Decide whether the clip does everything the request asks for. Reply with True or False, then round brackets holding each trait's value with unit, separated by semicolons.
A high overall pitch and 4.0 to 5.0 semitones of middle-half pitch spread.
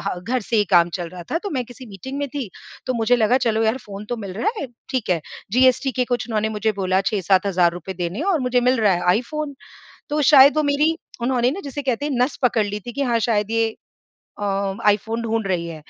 True (230 Hz; 4.6 semitones)